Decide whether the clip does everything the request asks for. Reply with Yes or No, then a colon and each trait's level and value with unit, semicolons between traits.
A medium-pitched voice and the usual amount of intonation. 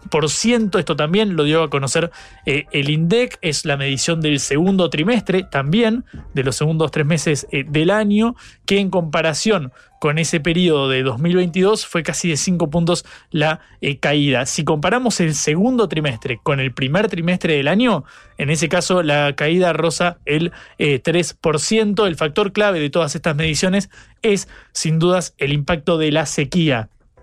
Yes: medium, 165 Hz; average, 3.6 semitones